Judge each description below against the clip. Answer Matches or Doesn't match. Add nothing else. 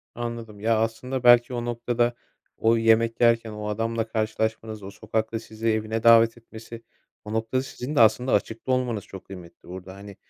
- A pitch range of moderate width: Doesn't match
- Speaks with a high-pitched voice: Doesn't match